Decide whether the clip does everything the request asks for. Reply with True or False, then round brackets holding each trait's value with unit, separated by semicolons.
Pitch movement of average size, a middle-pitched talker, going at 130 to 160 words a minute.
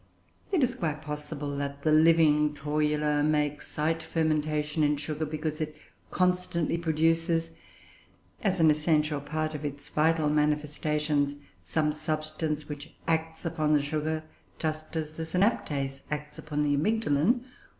False (1.4 semitones; 155 Hz; 135 wpm)